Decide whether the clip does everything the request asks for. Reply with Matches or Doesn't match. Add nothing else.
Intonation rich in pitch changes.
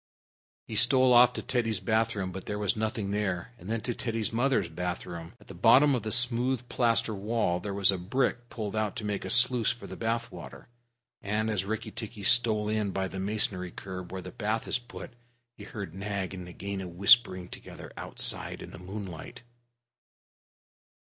Doesn't match